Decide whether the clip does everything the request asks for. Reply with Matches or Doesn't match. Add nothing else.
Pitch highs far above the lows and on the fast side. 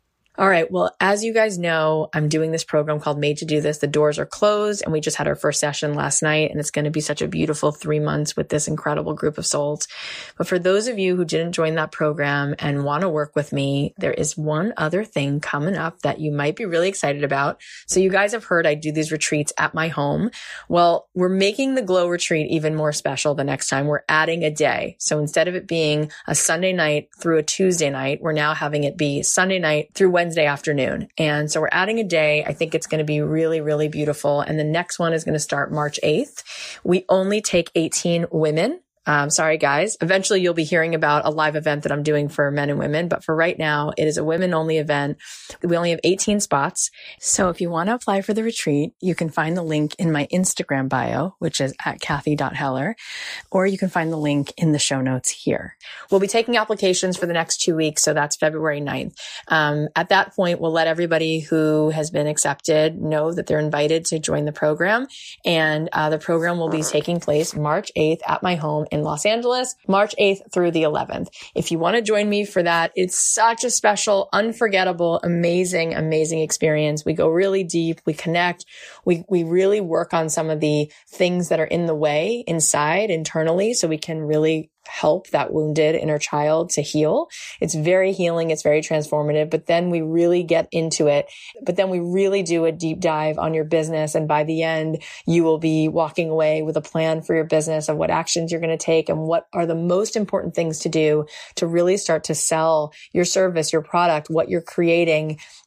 Doesn't match